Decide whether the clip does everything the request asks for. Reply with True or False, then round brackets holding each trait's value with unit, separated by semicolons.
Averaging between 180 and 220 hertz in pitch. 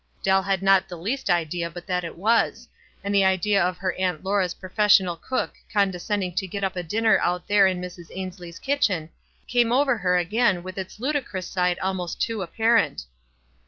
True (190 Hz)